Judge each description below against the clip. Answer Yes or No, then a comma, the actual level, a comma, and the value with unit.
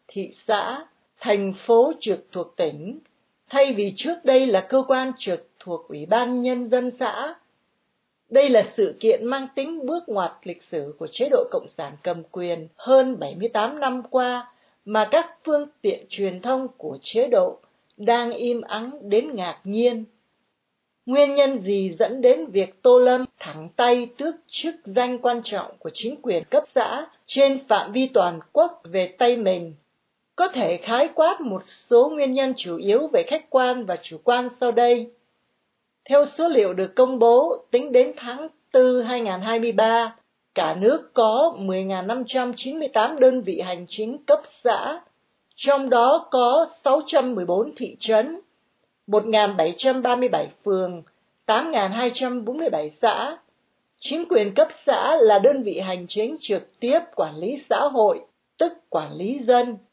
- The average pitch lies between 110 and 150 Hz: No, high, 245 Hz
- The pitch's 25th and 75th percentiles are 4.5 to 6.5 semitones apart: Yes, average, 5.2 semitones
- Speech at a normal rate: No, slow, 155 wpm